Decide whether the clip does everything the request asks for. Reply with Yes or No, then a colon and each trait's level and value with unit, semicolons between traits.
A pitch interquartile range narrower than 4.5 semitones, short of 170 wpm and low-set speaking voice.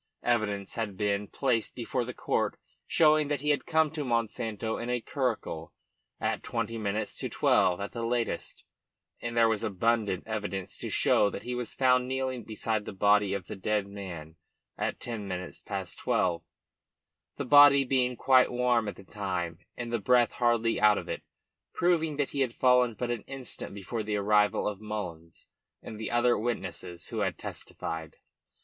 No: average, 3.7 semitones; average, 175 wpm; low, 115 Hz